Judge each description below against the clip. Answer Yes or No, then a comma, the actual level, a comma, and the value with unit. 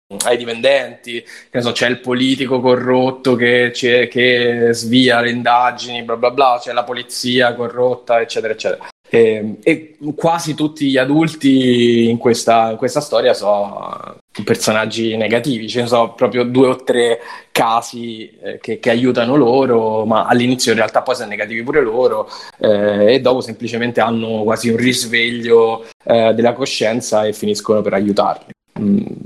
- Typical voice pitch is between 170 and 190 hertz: No, low, 120 Hz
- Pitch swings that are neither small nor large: No, narrow, 2.0 semitones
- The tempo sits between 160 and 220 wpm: No, average, 150 wpm